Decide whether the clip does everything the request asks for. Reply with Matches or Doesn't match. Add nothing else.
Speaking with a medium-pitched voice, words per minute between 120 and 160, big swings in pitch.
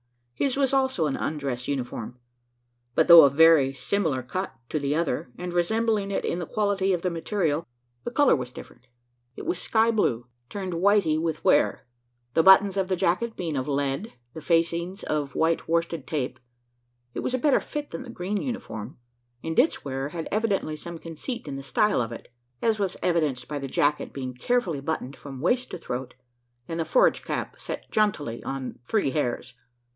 Doesn't match